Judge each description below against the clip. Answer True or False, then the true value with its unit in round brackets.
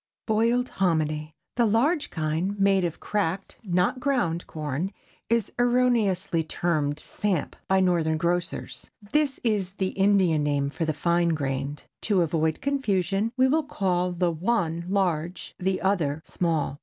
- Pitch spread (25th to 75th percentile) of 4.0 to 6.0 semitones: True (4.5 semitones)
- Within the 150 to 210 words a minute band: False (140 wpm)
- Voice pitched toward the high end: False (180 Hz)